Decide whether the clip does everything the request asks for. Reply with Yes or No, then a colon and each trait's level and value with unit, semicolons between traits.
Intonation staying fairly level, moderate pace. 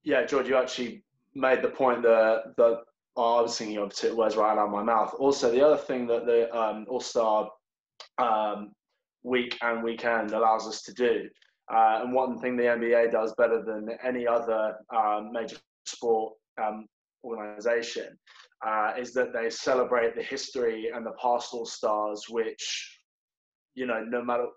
Yes: narrow, 2.3 semitones; average, 170 wpm